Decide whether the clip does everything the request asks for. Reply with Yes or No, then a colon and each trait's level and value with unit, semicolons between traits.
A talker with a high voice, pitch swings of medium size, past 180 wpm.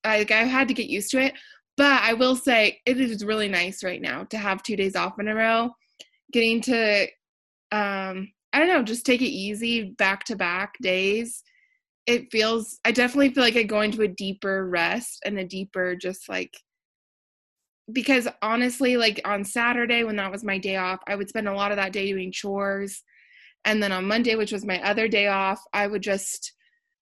Yes: high, 215 Hz; average, 3.5 semitones; average, 200 wpm